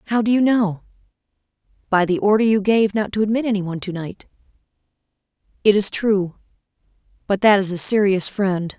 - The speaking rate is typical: Yes, average, 170 wpm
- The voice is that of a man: No, female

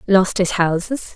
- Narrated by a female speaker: Yes, female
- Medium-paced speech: Yes, average, 155 wpm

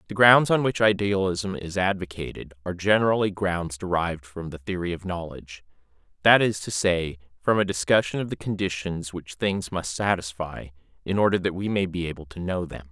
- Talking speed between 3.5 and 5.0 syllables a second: No, 5.4 syllables/s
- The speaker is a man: Yes, male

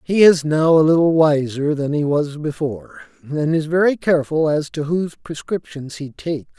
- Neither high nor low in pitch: Yes, medium, 155 Hz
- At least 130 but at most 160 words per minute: No, average, 180 wpm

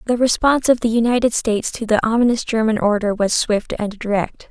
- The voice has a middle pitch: No, high, 225 Hz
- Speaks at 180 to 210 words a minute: Yes, average, 200 wpm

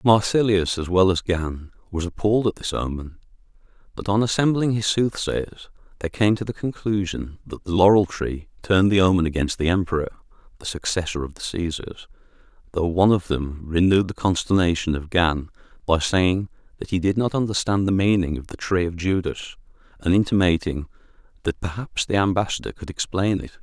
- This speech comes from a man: Yes, male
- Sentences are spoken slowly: No, average, 170 wpm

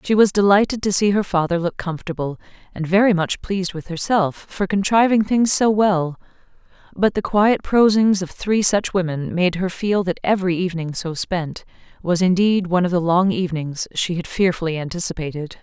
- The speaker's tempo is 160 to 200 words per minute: Yes, average, 180 wpm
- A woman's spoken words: Yes, female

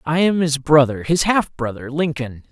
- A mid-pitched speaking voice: Yes, medium, 150 Hz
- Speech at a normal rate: Yes, average, 165 wpm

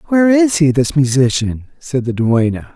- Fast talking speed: No, average, 175 wpm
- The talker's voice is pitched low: No, medium, 145 Hz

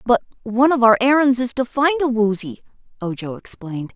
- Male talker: No, female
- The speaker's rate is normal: Yes, average, 180 wpm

